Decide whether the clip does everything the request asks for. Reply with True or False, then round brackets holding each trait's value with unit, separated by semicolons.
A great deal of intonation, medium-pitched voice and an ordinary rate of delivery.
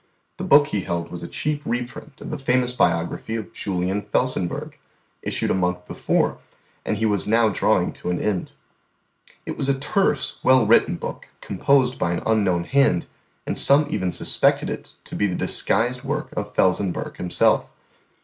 False (6.2 semitones; 110 Hz; 170 wpm)